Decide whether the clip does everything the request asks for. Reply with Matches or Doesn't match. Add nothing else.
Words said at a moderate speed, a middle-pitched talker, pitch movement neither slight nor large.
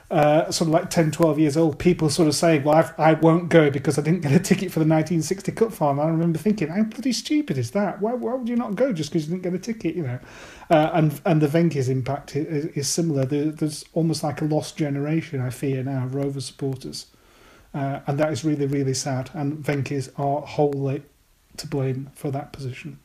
Doesn't match